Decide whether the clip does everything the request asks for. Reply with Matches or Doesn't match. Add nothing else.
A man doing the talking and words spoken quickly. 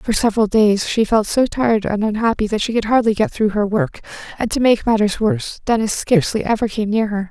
Doesn't match